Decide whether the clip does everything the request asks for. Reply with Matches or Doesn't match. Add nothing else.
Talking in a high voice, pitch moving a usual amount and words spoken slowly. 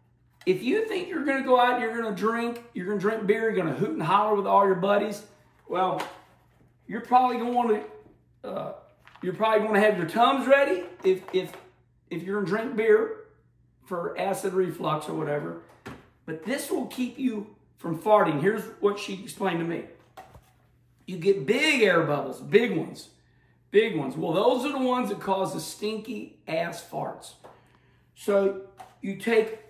Doesn't match